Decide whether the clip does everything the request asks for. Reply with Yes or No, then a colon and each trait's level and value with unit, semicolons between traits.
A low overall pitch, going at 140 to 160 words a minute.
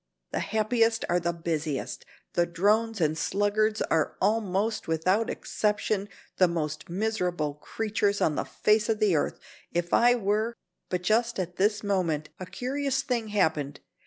No: high, 200 Hz; average, 155 wpm